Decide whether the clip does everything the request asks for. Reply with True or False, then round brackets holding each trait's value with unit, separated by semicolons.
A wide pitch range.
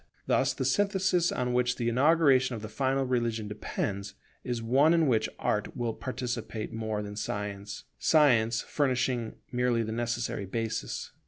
False (3.2 semitones)